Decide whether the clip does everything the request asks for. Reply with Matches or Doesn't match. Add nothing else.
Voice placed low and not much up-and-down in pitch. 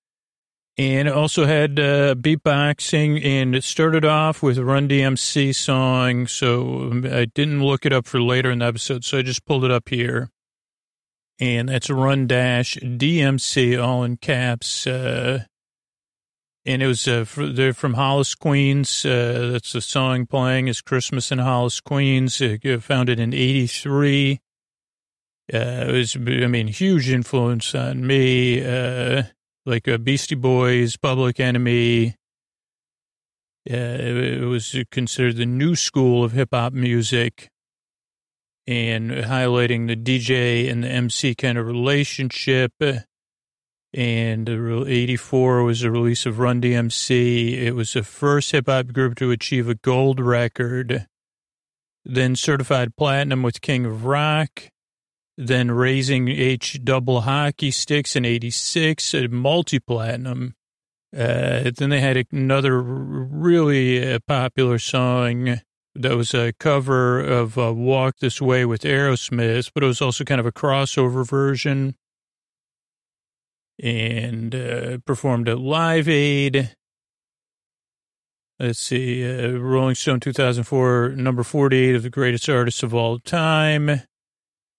Matches